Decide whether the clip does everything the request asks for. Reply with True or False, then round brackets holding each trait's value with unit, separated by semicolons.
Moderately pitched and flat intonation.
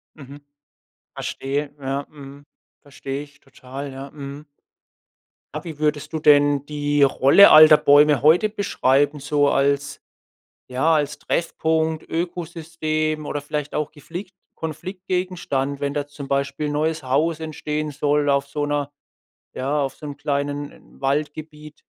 True (145 Hz; 1.7 semitones)